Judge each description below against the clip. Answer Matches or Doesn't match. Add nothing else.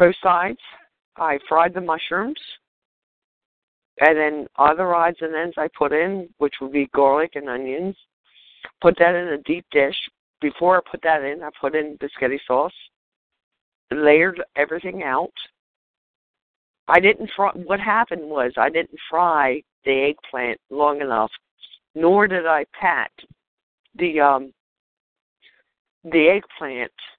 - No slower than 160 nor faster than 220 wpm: Doesn't match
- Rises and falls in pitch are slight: Doesn't match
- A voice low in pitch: Doesn't match